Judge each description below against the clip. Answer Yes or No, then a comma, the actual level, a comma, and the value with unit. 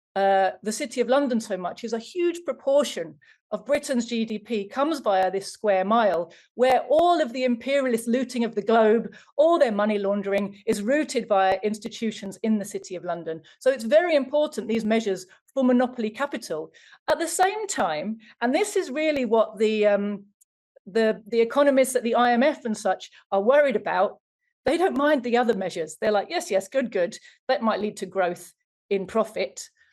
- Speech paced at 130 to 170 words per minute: No, average, 180 wpm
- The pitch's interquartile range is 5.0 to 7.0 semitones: Yes, wide, 5.6 semitones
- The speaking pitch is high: Yes, high, 225 Hz